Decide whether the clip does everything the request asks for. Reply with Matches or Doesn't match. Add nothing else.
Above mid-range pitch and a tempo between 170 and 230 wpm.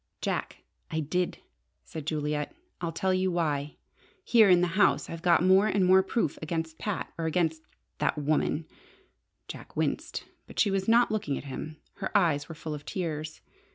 Doesn't match